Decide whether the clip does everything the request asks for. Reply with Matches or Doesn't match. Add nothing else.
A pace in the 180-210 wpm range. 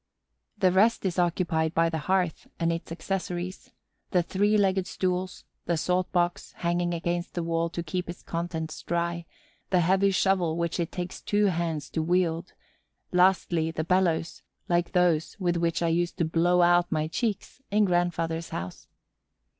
Doesn't match